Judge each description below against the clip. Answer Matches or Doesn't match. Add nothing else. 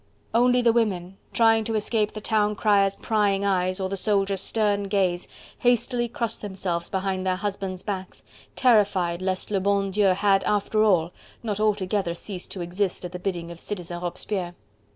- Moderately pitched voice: Doesn't match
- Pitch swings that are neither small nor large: Doesn't match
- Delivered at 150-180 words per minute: Matches